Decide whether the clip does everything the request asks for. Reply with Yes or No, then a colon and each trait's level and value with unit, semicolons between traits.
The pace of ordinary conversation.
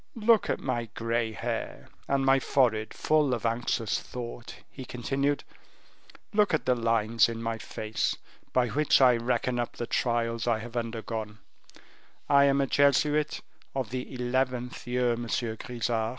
Yes: average, 150 wpm